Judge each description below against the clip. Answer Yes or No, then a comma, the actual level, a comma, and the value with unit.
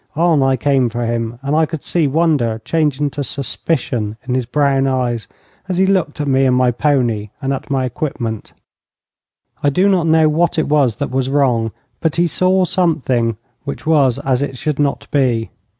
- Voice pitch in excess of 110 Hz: Yes, medium, 140 Hz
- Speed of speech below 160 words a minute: No, average, 195 wpm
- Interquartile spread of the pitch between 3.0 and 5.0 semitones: Yes, average, 3.9 semitones